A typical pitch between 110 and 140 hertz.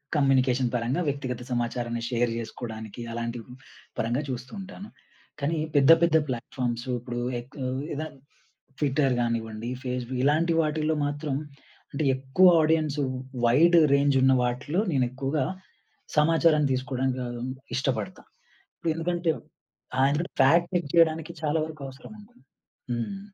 Yes: low, 135 Hz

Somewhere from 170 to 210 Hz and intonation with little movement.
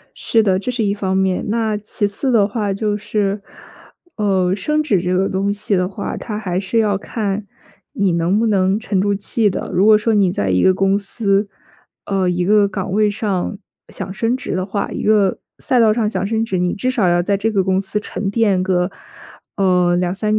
Yes: high, 200 Hz; narrow, 2.2 semitones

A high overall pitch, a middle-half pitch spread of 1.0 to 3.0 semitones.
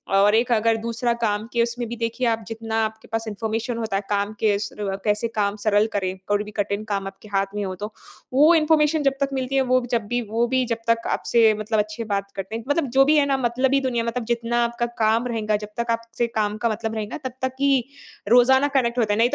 Yes: high, 230 Hz; narrow, 2.5 semitones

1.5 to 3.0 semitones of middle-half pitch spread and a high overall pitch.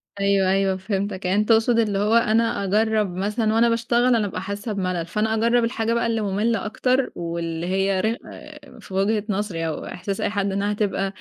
Yes: average, 2.7 semitones; high, 205 Hz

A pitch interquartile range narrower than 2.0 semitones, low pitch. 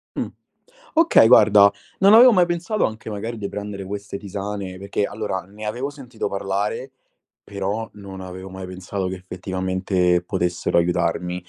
No: average, 2.8 semitones; low, 100 Hz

